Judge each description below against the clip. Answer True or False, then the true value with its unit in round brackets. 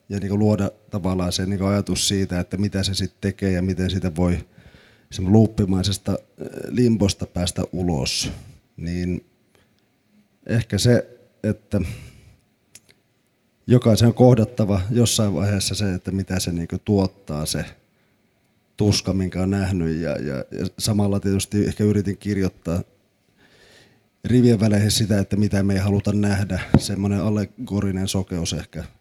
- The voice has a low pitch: True (100 Hz)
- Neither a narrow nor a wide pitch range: False (2.1 semitones)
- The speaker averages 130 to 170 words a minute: False (120 wpm)